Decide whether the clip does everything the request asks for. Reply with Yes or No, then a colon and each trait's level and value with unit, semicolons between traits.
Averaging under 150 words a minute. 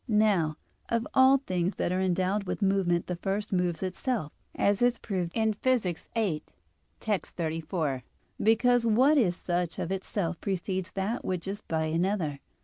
No: average, 155 wpm